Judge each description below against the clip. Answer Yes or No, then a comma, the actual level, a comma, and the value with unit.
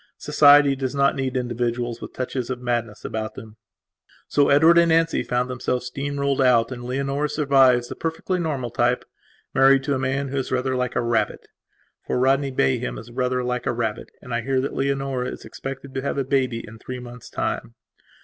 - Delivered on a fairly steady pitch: Yes, narrow, 2.2 semitones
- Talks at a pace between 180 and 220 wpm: Yes, average, 195 wpm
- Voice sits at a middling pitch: No, low, 130 Hz